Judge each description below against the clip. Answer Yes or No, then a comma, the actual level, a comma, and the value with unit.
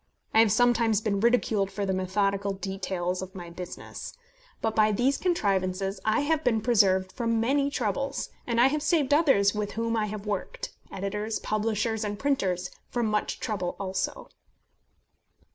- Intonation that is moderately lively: Yes, average, 3.4 semitones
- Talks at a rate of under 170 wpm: Yes, average, 160 wpm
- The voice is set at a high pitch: Yes, high, 210 Hz